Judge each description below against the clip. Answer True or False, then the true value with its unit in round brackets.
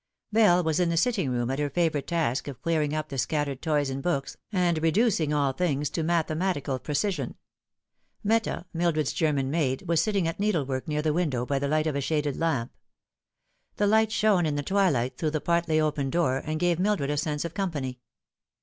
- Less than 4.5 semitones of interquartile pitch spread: True (3.6 semitones)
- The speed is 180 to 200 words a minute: True (195 wpm)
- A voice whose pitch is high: False (155 Hz)